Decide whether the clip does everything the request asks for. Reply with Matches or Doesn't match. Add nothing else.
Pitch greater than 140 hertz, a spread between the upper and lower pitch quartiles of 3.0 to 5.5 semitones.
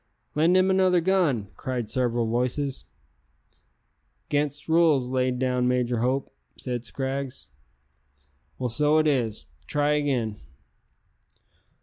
Doesn't match